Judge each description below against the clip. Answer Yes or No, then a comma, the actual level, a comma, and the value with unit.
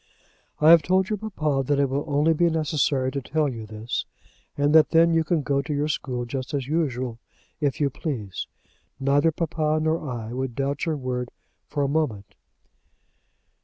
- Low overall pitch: No, medium, 145 Hz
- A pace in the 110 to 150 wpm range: No, average, 180 wpm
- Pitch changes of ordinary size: Yes, average, 3.4 semitones